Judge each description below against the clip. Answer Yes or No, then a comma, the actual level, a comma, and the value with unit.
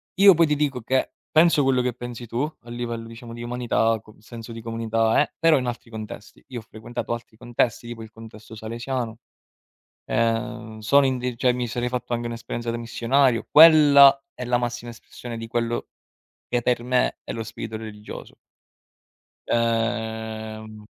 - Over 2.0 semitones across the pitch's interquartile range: No, narrow, 1.7 semitones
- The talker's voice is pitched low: Yes, low, 120 Hz